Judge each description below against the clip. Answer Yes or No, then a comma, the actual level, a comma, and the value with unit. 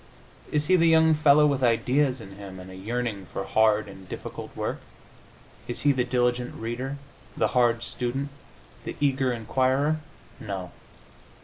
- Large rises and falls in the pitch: No, average, 4.4 semitones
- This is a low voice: Yes, low, 125 Hz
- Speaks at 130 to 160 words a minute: Yes, average, 150 wpm